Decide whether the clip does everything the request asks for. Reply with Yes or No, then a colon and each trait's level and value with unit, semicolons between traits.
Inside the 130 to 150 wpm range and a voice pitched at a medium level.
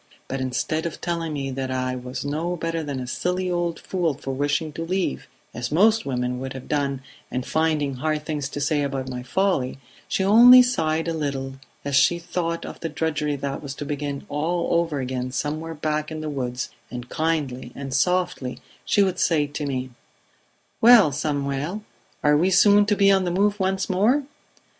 No: average, 190 wpm; medium, 150 Hz